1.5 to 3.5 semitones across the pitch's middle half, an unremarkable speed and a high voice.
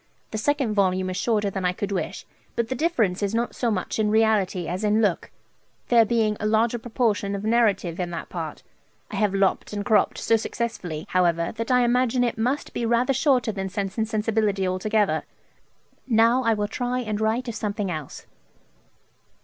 Yes: average, 3.2 semitones; average, 190 wpm; high, 215 Hz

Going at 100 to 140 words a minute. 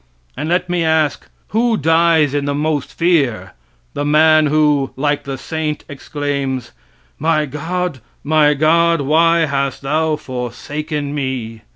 Yes: slow, 135 wpm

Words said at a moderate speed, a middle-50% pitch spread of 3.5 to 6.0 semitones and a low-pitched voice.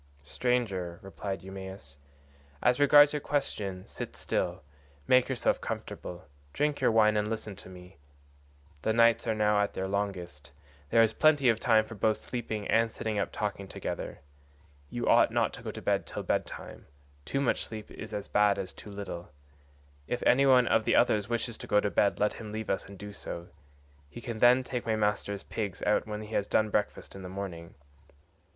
No: average, 195 wpm; average, 3.0 semitones; low, 105 Hz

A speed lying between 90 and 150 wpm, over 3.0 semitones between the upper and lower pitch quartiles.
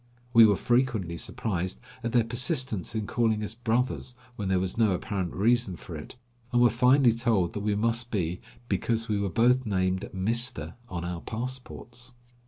No: average, 175 wpm; average, 4.3 semitones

